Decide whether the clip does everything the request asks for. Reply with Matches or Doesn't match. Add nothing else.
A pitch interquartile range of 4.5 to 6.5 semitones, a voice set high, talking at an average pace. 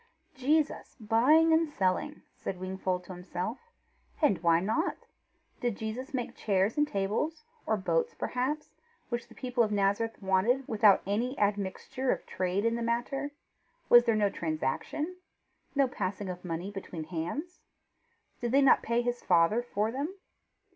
Matches